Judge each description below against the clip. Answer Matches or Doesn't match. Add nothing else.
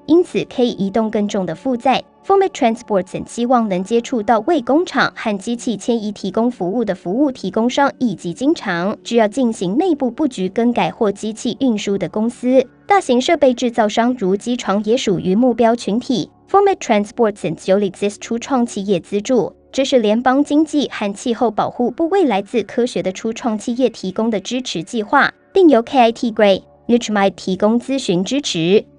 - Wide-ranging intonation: Doesn't match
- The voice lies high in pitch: Matches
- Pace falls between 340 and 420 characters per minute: Matches